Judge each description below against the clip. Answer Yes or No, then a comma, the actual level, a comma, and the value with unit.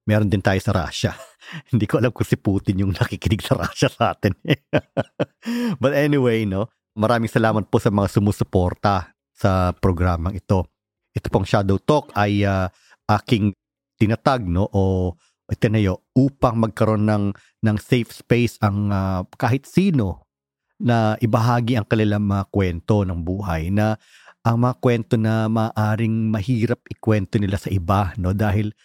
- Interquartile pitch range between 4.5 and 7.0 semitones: No, average, 3.4 semitones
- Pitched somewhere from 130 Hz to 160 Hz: No, low, 105 Hz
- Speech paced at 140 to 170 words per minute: Yes, average, 150 wpm